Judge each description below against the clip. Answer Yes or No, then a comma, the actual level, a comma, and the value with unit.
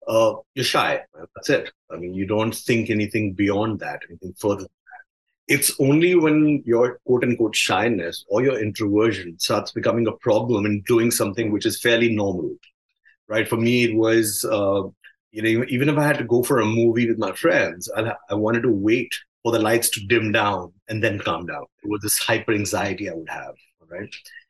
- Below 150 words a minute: No, average, 200 wpm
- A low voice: Yes, low, 115 Hz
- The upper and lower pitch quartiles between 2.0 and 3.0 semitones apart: Yes, narrow, 2.6 semitones